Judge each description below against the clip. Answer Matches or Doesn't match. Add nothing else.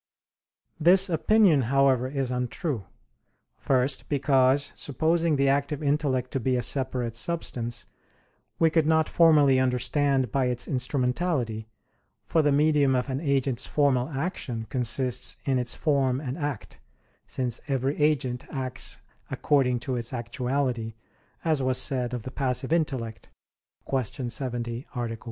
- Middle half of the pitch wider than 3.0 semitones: Doesn't match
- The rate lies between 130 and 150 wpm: Matches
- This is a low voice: Matches